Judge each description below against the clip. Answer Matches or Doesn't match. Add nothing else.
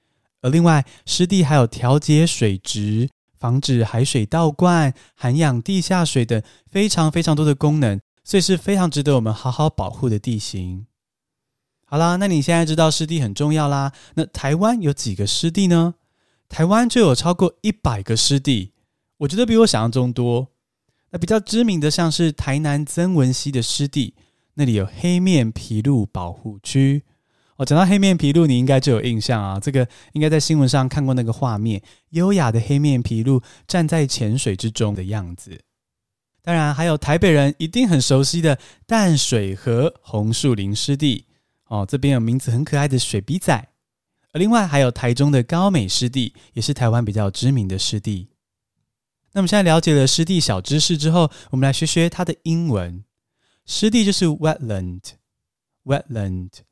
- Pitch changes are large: Matches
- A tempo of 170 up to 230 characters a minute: Doesn't match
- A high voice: Doesn't match